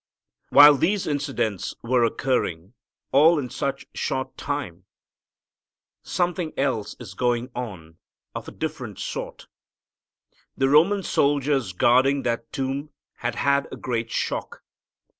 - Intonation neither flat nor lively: Yes, average, 3.7 semitones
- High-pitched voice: No, low, 135 Hz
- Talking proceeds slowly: Yes, slow, 120 wpm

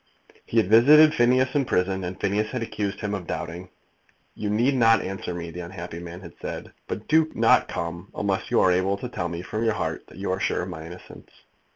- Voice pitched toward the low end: Yes, low, 100 Hz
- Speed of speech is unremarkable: No, fast, 225 wpm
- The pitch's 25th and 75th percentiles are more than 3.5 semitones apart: Yes, average, 4.3 semitones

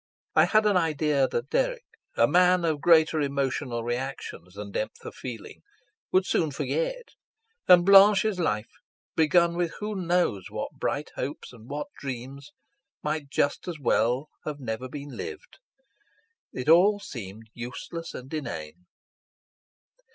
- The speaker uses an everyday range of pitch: No, wide, 6.1 semitones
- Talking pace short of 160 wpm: Yes, slow, 135 wpm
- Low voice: No, medium, 150 Hz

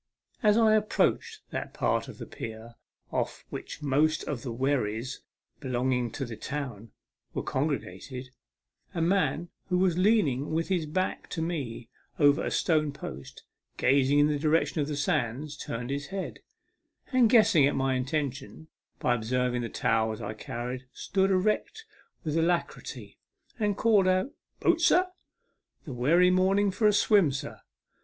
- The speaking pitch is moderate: Yes, medium, 150 Hz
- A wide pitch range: Yes, wide, 6.5 semitones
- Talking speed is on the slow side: No, average, 155 wpm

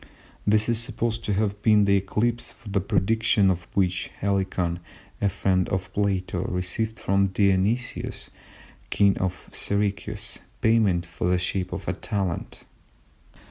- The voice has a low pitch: Yes, low, 100 Hz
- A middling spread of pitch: No, narrow, 2.3 semitones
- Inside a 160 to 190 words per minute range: No, average, 140 wpm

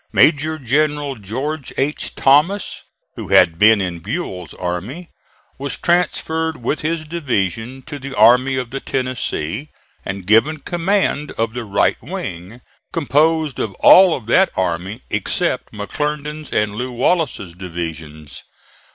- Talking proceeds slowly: Yes, slow, 130 wpm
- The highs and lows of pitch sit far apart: Yes, wide, 7.1 semitones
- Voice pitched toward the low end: Yes, low, 130 Hz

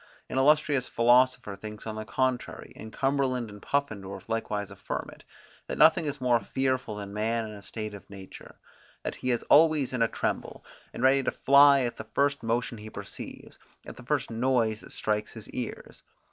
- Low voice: Yes, low, 120 Hz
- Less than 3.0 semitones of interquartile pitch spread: No, average, 3.7 semitones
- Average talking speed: Yes, average, 190 wpm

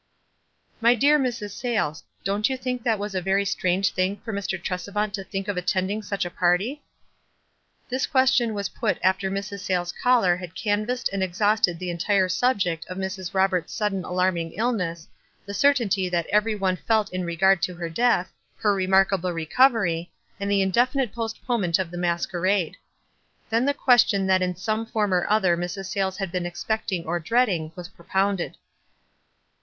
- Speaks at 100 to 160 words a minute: No, average, 170 wpm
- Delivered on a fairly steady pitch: No, average, 3.2 semitones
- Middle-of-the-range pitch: No, high, 195 Hz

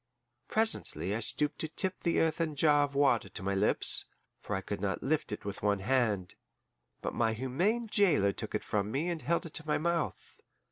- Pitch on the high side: No, medium, 140 Hz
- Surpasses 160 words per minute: Yes, average, 200 wpm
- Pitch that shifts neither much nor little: No, wide, 7.9 semitones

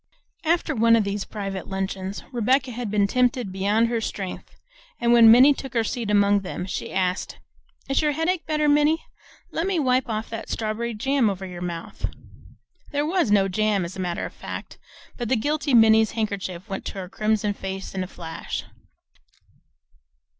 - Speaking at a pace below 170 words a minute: No, average, 175 wpm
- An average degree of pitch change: Yes, average, 4.8 semitones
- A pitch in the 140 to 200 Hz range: No, high, 220 Hz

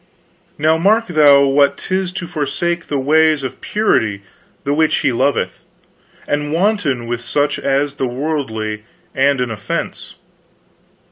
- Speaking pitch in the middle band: Yes, medium, 145 Hz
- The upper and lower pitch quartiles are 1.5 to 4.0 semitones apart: Yes, average, 3.4 semitones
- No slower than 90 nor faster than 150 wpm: Yes, slow, 135 wpm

